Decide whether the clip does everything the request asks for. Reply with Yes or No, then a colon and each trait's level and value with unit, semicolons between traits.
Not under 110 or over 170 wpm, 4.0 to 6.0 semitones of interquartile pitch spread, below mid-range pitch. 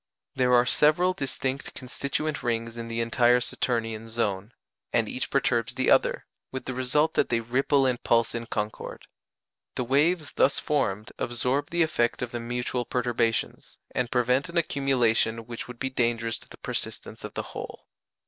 No: average, 165 wpm; average, 2.8 semitones; low, 125 Hz